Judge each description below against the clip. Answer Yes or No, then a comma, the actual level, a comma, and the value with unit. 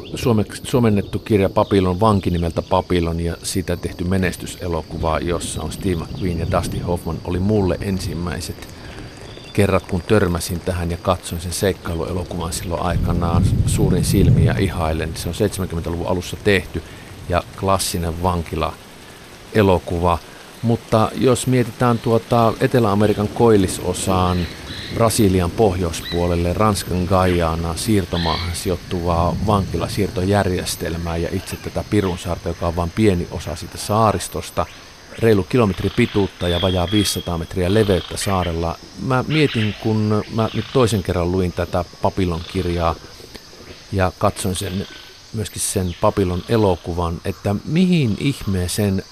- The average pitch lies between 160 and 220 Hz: No, very low, 95 Hz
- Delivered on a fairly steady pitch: No, average, 3.3 semitones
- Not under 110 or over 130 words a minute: Yes, average, 115 wpm